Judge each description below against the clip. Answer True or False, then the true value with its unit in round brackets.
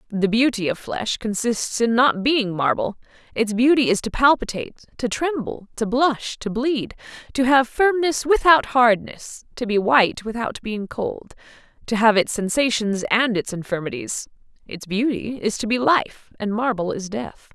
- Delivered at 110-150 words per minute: False (165 wpm)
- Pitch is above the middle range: True (230 Hz)